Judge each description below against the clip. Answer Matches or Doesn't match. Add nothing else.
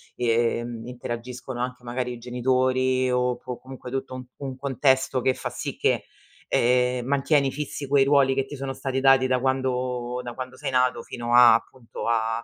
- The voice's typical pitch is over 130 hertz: Doesn't match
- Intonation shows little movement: Matches